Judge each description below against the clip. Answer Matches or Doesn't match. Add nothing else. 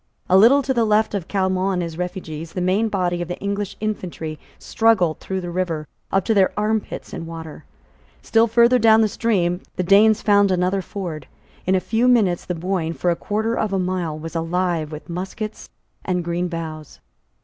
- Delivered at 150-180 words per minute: Doesn't match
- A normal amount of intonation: Matches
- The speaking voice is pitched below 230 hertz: Matches